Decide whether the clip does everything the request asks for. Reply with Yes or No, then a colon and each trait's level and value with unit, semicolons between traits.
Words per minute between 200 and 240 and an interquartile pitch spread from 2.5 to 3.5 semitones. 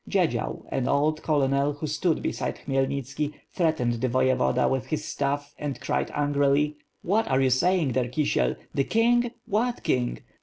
No: average, 160 wpm; average, 2.8 semitones